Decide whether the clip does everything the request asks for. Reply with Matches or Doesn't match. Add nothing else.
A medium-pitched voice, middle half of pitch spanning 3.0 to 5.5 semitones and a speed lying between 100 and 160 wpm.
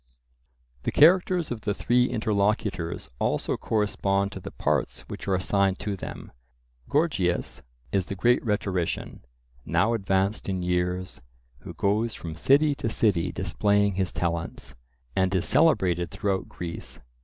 Doesn't match